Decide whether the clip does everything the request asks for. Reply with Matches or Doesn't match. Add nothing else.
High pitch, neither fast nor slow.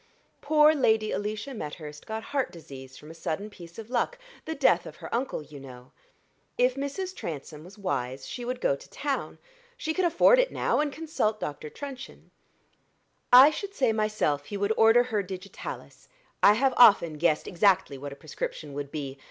Matches